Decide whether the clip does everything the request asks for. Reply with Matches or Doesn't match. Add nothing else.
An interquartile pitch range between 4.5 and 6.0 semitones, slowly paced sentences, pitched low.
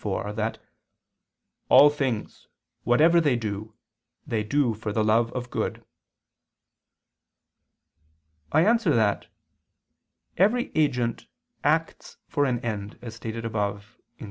Matches